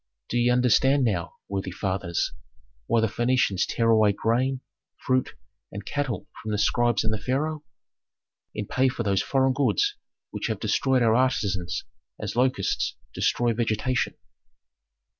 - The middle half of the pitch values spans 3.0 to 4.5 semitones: Yes, average, 3.9 semitones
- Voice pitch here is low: Yes, low, 120 Hz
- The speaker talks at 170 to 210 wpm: No, average, 140 wpm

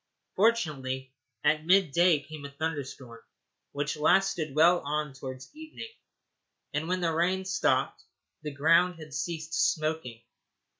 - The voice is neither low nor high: Yes, medium, 155 Hz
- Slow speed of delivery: Yes, slow, 130 wpm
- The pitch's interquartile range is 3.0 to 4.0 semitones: Yes, average, 3.7 semitones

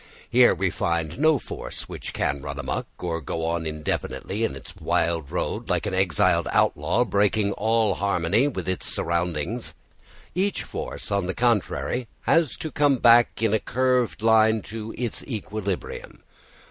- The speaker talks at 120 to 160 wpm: Yes, average, 155 wpm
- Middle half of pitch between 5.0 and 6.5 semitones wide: Yes, wide, 5.5 semitones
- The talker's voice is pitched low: Yes, low, 105 Hz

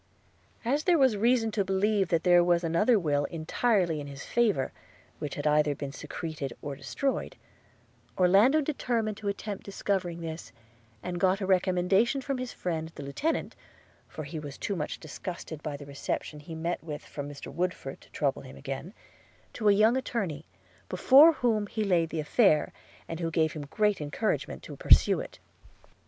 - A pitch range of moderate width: No, wide, 5.9 semitones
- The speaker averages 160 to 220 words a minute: Yes, average, 175 wpm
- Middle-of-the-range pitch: Yes, medium, 175 Hz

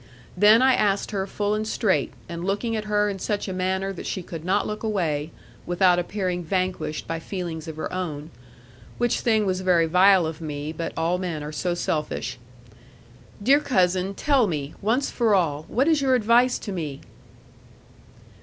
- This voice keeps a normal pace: Yes, average, 180 wpm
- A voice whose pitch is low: No, medium, 185 Hz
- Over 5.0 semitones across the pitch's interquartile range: No, average, 4.2 semitones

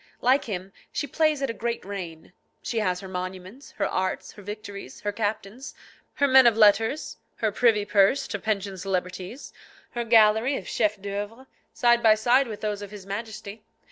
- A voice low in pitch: No, high, 210 Hz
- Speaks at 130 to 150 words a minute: No, average, 175 wpm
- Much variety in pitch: No, average, 3.2 semitones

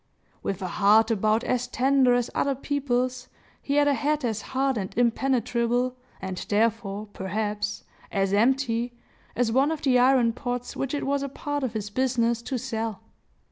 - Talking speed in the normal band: Yes, average, 170 wpm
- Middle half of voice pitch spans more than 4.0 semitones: No, average, 3.4 semitones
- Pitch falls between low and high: No, high, 245 Hz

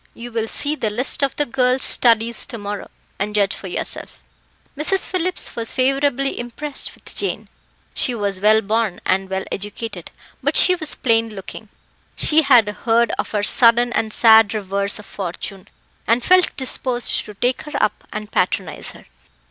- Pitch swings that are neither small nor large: Yes, average, 3.9 semitones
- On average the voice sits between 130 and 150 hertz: No, high, 230 Hz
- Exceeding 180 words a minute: No, average, 170 wpm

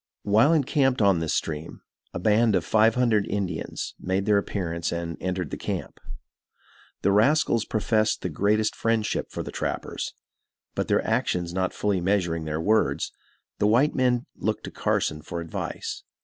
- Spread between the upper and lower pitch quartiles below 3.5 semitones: No, average, 4.5 semitones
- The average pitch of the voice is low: Yes, low, 100 Hz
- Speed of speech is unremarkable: Yes, average, 160 wpm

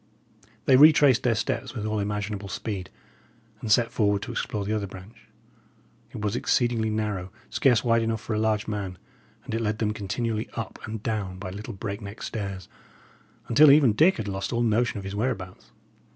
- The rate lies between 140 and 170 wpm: No, average, 185 wpm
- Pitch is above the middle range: No, low, 110 Hz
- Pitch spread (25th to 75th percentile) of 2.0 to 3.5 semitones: Yes, narrow, 2.5 semitones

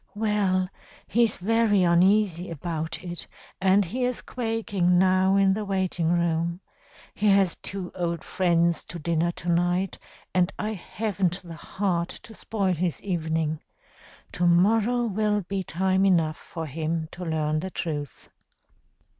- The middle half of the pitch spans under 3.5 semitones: Yes, average, 2.8 semitones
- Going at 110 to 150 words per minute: Yes, average, 140 wpm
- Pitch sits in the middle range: Yes, medium, 180 Hz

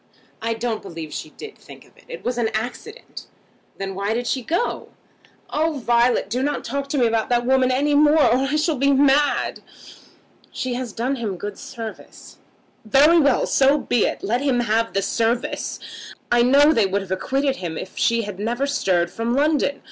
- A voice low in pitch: No, high, 245 Hz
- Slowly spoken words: No, average, 195 wpm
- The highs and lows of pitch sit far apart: No, average, 4.1 semitones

